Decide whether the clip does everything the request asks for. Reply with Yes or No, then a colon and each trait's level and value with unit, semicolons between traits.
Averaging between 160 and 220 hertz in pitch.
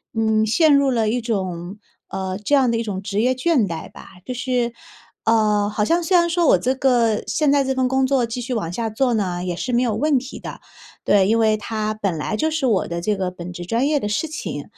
No: high, 230 Hz